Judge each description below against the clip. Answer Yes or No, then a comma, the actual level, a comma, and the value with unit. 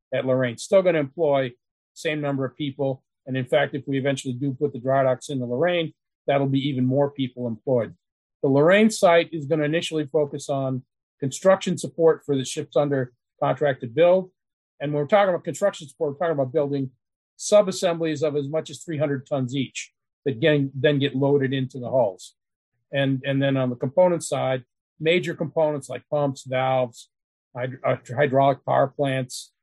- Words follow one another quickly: No, average, 190 wpm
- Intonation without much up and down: No, average, 3.2 semitones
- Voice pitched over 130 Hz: Yes, medium, 140 Hz